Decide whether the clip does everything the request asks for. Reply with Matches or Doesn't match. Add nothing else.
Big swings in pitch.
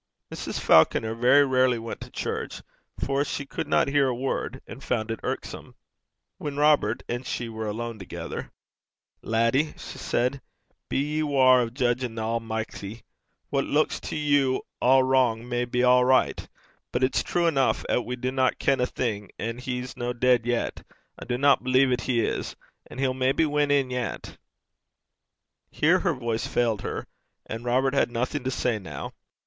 Doesn't match